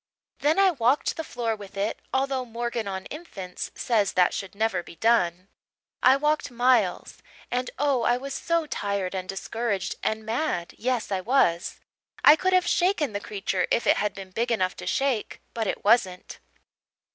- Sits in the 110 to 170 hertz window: No, high, 230 Hz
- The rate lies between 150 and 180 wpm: Yes, average, 175 wpm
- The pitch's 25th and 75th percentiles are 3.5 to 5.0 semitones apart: No, wide, 5.5 semitones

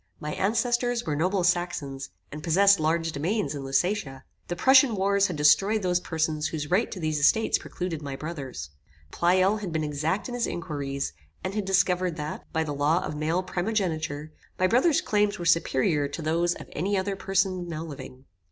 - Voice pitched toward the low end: No, medium, 170 Hz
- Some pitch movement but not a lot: Yes, average, 4.3 semitones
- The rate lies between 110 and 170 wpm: No, average, 180 wpm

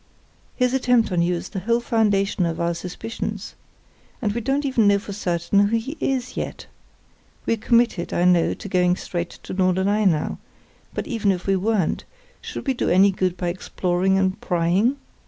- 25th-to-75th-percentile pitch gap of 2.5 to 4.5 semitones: Yes, average, 4.2 semitones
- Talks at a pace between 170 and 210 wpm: Yes, average, 180 wpm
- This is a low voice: No, high, 195 Hz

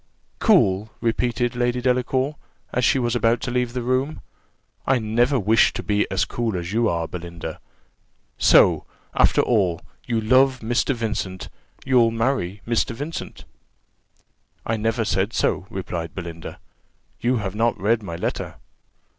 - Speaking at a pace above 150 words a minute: No, average, 145 wpm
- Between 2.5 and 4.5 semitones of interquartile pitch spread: Yes, average, 4.0 semitones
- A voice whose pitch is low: Yes, low, 115 Hz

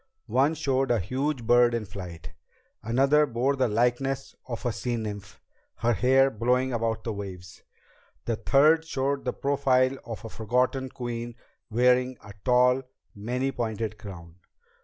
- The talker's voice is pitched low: Yes, low, 120 Hz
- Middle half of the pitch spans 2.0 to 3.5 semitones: Yes, average, 3.2 semitones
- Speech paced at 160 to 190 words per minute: No, average, 145 wpm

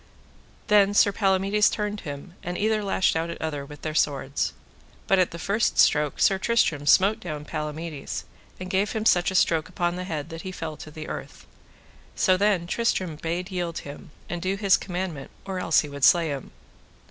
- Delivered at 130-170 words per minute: No, average, 190 wpm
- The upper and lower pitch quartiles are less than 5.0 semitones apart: Yes, average, 3.9 semitones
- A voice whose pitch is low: No, medium, 175 Hz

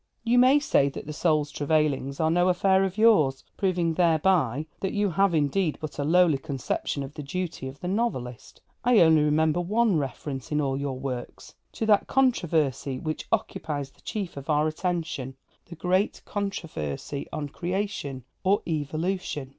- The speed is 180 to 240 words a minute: No, average, 165 wpm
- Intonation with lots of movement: No, average, 5.0 semitones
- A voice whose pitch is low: No, medium, 160 Hz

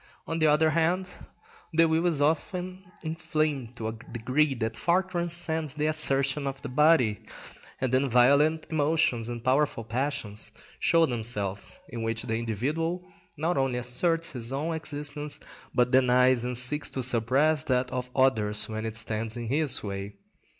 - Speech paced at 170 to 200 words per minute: No, average, 155 wpm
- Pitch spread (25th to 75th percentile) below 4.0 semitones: No, average, 4.9 semitones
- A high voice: No, low, 135 Hz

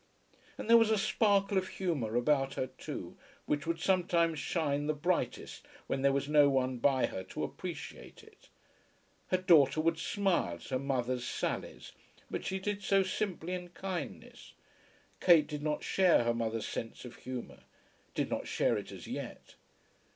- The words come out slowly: No, average, 165 wpm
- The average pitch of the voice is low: No, medium, 155 Hz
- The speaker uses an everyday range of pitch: No, wide, 5.8 semitones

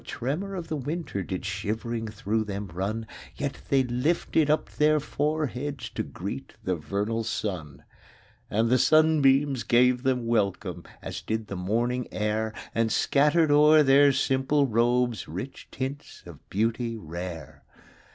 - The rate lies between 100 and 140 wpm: No, average, 150 wpm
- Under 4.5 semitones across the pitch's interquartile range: No, average, 5.1 semitones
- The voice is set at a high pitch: No, low, 120 Hz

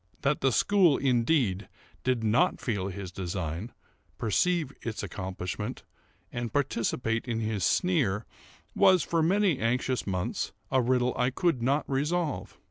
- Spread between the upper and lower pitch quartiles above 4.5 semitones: Yes, average, 5.3 semitones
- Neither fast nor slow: No, slow, 130 wpm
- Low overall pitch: Yes, low, 125 Hz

